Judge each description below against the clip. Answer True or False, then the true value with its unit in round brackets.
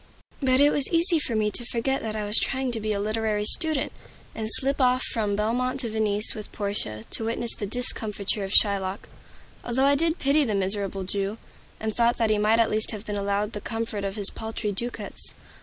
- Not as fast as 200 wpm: False (205 wpm)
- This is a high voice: True (220 Hz)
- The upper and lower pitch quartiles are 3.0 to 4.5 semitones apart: True (3.3 semitones)